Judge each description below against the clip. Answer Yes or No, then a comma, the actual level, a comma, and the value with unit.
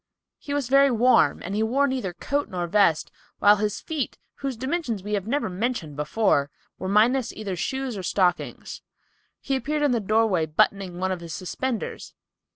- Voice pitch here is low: No, high, 215 Hz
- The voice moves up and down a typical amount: No, wide, 6.0 semitones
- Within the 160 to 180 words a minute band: Yes, average, 170 wpm